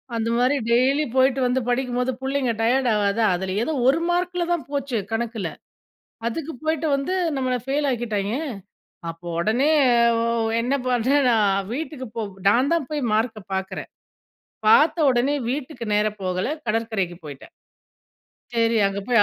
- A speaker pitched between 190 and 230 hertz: No, high, 245 Hz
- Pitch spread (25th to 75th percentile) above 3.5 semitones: Yes, average, 4.2 semitones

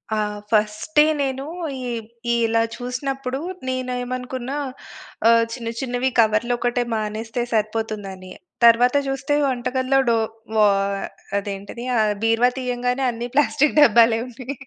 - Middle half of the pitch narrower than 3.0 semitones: Yes, narrow, 2.5 semitones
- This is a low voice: No, high, 245 Hz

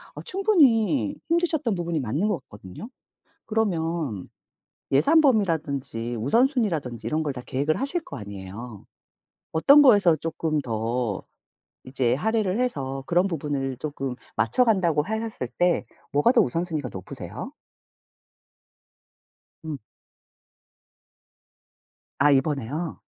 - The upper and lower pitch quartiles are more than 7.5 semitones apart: Yes, wide, 8.8 semitones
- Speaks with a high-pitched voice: No, medium, 160 Hz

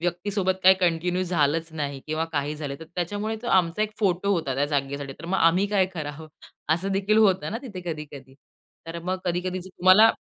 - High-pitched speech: No, medium, 175 Hz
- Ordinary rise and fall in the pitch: Yes, average, 3.6 semitones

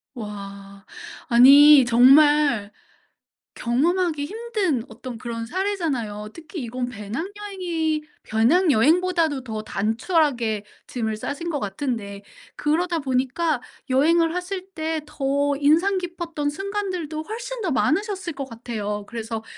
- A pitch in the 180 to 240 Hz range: No, very high, 290 Hz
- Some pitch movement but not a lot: No, wide, 6.8 semitones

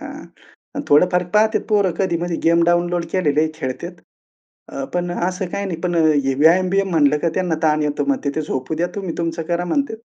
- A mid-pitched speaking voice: Yes, medium, 175 Hz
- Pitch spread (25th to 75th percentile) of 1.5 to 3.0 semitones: Yes, average, 2.7 semitones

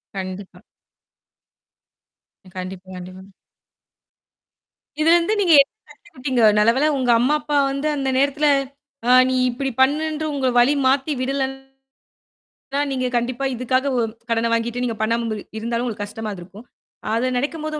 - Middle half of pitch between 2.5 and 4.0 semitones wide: Yes, average, 3.7 semitones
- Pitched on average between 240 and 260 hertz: Yes, very high, 255 Hz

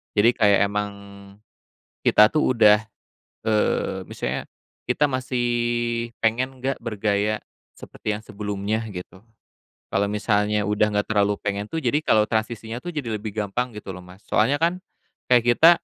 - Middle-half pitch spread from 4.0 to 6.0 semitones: No, average, 2.9 semitones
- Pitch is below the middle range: Yes, low, 110 Hz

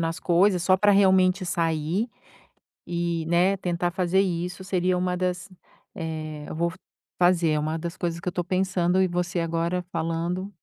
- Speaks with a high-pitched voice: No, medium, 175 Hz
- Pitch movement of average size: No, narrow, 1.6 semitones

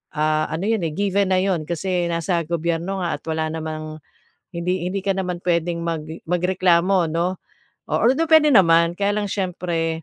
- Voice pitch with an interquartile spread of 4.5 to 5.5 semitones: No, narrow, 2.5 semitones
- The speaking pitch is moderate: Yes, medium, 175 Hz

